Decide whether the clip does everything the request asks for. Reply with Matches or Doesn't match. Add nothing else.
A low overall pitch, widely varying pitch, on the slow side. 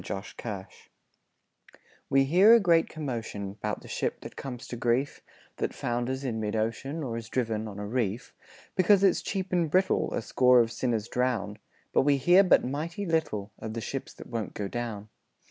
Doesn't match